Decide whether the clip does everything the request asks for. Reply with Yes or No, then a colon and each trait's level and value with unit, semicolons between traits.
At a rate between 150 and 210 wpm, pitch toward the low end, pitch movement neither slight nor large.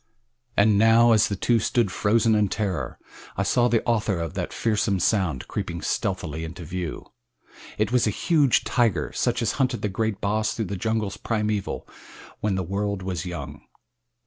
Yes: average, 170 wpm; low, 105 Hz; average, 3.4 semitones